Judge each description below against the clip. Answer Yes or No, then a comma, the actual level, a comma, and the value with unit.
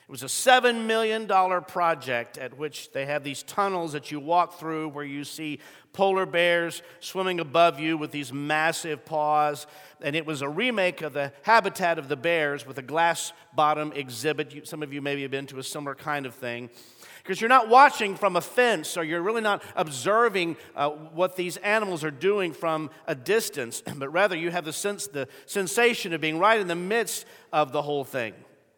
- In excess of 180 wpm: Yes, average, 200 wpm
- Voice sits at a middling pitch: Yes, medium, 165 Hz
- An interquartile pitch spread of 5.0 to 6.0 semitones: No, average, 4.2 semitones